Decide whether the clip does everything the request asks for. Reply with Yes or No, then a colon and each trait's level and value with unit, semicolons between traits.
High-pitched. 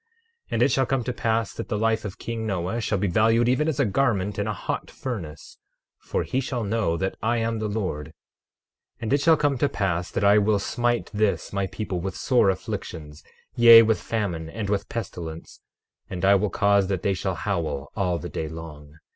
No: low, 105 Hz